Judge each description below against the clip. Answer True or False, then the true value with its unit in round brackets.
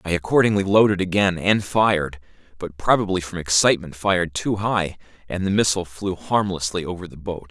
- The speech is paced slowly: False (170 wpm)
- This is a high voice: False (95 Hz)